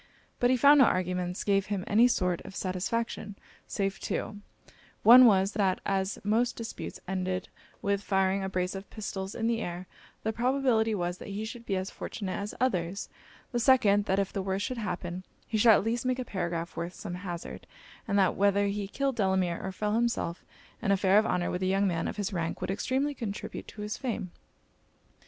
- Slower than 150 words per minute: No, average, 200 wpm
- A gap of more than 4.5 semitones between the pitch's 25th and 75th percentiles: No, average, 3.3 semitones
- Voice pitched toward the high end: Yes, high, 200 Hz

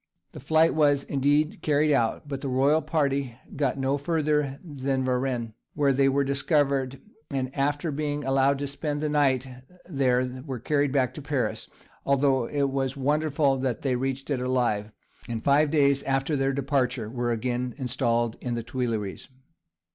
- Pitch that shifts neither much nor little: No, narrow, 2.2 semitones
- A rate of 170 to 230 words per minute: No, average, 160 wpm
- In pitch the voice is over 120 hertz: Yes, low, 135 Hz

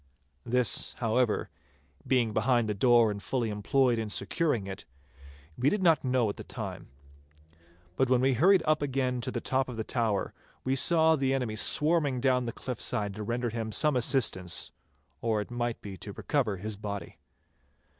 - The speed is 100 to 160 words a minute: No, average, 175 wpm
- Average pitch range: Yes, average, 3.6 semitones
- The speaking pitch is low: Yes, low, 120 Hz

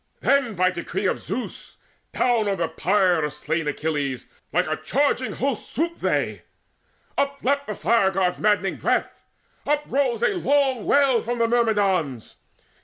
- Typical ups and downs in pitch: No, wide, 7.1 semitones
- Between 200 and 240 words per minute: No, average, 145 wpm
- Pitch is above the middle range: Yes, high, 215 Hz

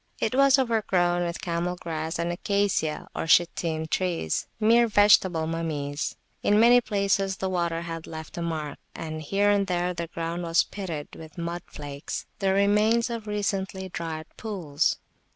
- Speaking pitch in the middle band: Yes, medium, 175 Hz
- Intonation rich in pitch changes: No, average, 3.7 semitones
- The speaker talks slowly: No, average, 150 wpm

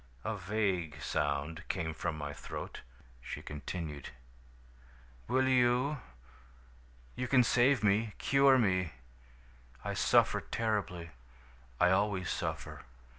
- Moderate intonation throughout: No, wide, 6.7 semitones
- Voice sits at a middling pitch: No, low, 100 Hz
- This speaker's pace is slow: Yes, slow, 105 wpm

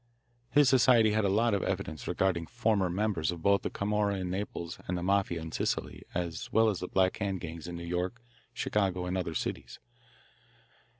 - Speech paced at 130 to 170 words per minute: No, average, 190 wpm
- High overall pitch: No, very low, 95 Hz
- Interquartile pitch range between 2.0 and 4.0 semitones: Yes, average, 3.3 semitones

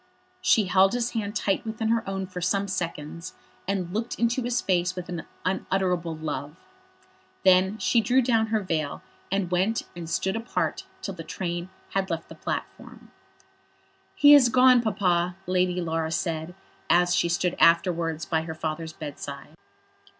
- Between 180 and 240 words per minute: No, average, 155 wpm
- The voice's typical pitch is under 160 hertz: No, medium, 185 Hz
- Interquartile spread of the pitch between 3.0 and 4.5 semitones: Yes, average, 4.2 semitones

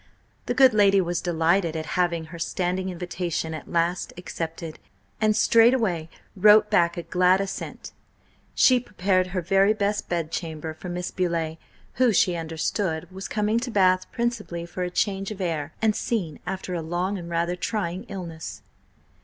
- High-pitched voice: No, medium, 180 Hz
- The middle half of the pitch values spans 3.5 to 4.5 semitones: No, average, 3.0 semitones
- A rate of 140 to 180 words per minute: Yes, average, 160 wpm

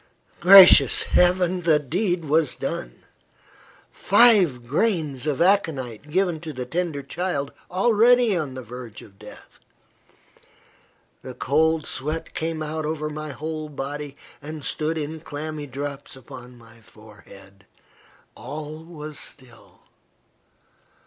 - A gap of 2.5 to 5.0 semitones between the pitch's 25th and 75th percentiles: Yes, average, 4.1 semitones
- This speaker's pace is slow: Yes, slow, 115 wpm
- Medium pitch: Yes, medium, 150 Hz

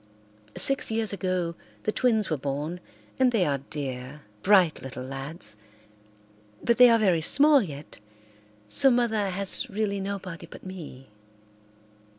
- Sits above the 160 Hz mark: Yes, medium, 185 Hz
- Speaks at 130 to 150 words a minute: Yes, slow, 135 wpm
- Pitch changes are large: Yes, wide, 6.9 semitones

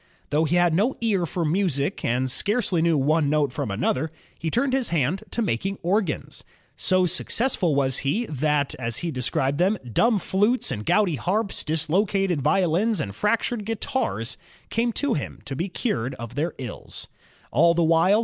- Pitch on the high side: No, medium, 170 Hz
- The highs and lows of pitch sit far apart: Yes, wide, 6.3 semitones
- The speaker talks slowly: No, average, 160 wpm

